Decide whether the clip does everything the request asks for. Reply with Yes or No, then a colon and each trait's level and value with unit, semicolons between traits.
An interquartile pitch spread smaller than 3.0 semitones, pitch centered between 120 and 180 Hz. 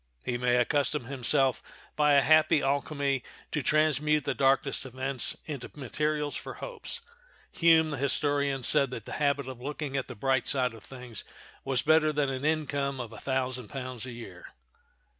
Yes: narrow, 2.6 semitones; low, 135 Hz